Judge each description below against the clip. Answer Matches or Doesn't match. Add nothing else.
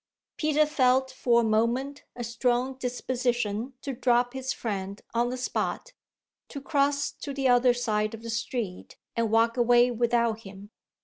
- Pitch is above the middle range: Matches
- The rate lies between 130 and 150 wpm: Doesn't match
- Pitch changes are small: Matches